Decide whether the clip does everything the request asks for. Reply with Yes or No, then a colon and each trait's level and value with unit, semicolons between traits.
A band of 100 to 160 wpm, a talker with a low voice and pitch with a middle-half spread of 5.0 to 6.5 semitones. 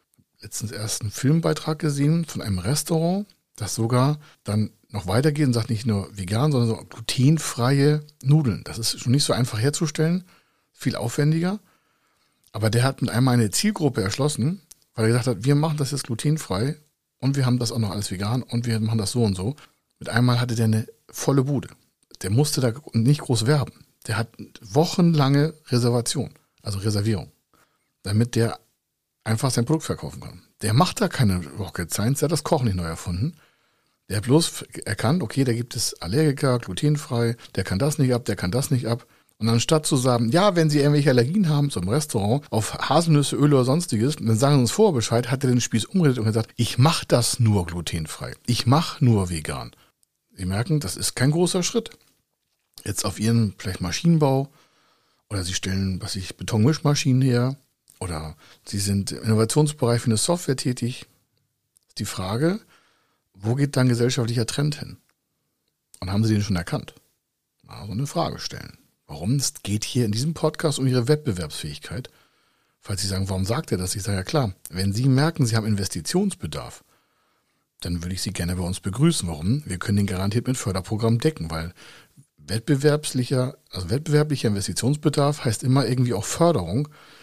No: average, 180 wpm; low, 120 Hz; average, 5.3 semitones